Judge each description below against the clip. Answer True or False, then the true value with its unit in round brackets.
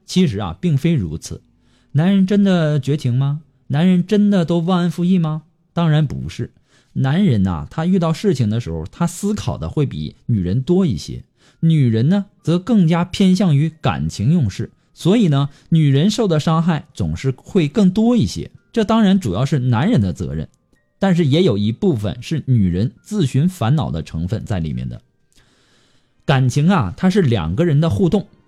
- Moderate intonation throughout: False (6.8 semitones)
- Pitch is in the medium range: True (155 Hz)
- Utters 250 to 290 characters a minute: True (255 characters per minute)